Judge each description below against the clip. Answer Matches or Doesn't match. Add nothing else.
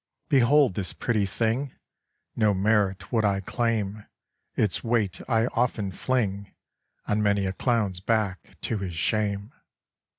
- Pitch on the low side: Matches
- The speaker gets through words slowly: Matches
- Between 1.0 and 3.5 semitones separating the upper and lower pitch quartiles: Matches